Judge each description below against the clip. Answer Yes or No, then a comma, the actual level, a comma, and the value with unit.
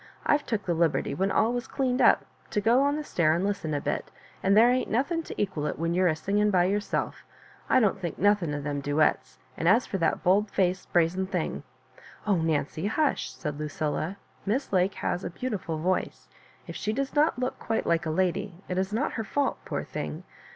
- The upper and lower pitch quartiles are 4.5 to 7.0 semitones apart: Yes, average, 5.0 semitones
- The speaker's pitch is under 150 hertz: No, high, 190 Hz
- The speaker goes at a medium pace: No, fast, 220 wpm